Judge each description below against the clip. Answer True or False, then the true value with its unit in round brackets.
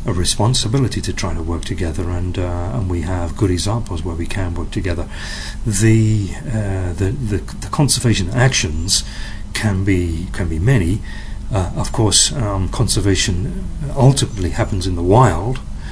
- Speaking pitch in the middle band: False (100 Hz)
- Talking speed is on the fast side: False (155 wpm)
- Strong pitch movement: False (4.2 semitones)